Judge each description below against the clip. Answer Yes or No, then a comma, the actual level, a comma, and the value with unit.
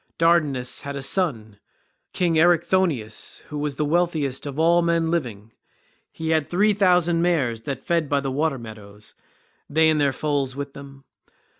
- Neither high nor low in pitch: Yes, medium, 150 Hz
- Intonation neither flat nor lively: Yes, average, 4.0 semitones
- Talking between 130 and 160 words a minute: Yes, average, 155 wpm